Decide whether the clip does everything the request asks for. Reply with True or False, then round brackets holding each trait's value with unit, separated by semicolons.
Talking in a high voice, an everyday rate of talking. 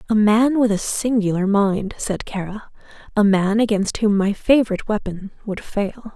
True (210 Hz; 165 wpm)